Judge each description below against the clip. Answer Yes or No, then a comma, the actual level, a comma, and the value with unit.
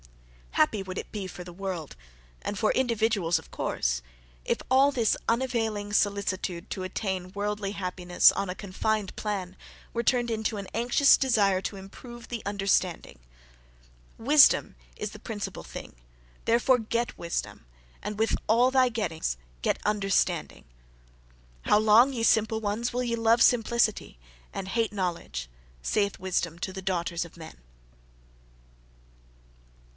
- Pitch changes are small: No, average, 3.7 semitones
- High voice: Yes, high, 205 Hz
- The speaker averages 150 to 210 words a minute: No, average, 140 wpm